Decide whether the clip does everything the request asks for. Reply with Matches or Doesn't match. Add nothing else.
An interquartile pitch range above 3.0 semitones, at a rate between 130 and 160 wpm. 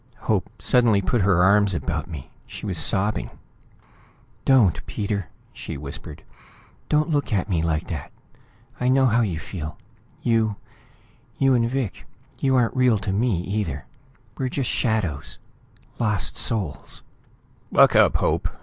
Matches